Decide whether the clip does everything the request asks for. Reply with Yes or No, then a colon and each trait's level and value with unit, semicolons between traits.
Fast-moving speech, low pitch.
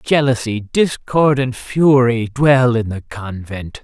No: slow, 125 wpm; low, 125 Hz